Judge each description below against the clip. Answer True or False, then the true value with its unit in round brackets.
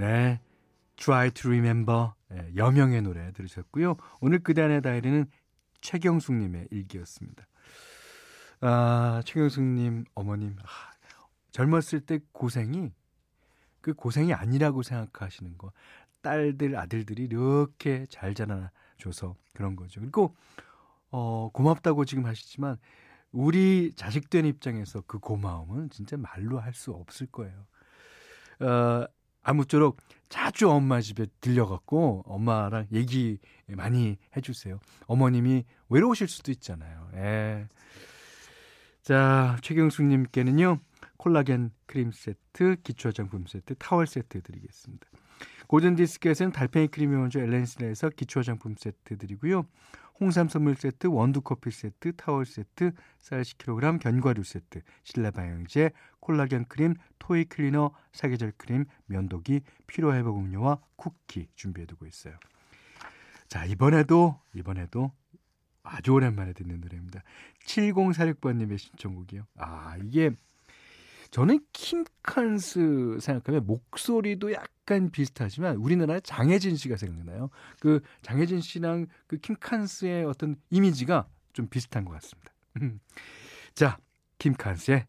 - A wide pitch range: True (6.2 semitones)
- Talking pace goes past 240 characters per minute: True (280 characters per minute)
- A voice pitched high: False (130 Hz)